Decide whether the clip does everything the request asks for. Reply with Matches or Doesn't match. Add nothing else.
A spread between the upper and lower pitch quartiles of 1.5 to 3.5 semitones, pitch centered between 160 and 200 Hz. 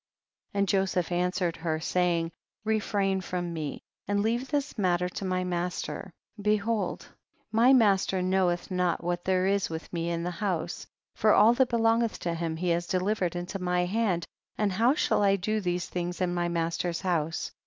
Matches